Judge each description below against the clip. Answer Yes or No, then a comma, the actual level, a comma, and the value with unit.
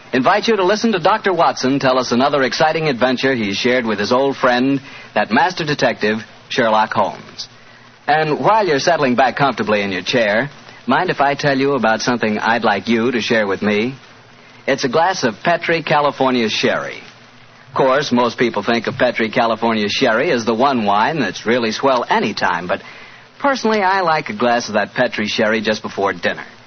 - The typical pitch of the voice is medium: No, low, 125 Hz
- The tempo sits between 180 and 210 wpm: Yes, average, 185 wpm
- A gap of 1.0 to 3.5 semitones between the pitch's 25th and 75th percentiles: No, average, 4.2 semitones